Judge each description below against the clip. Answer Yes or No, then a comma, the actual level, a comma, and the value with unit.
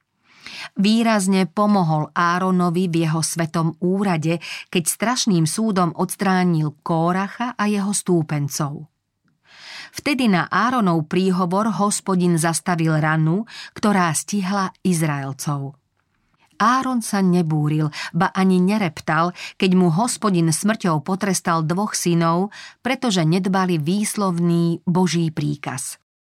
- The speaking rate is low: Yes, slow, 100 wpm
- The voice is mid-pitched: Yes, medium, 180 Hz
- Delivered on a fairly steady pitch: No, average, 3.3 semitones